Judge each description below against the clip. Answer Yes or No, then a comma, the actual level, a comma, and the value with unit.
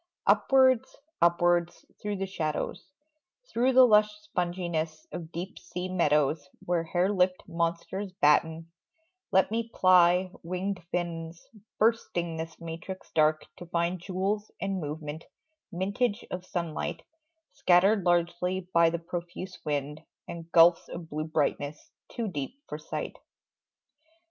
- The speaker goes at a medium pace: No, slow, 125 wpm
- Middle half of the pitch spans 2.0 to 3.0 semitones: Yes, narrow, 2.6 semitones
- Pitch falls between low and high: Yes, medium, 175 Hz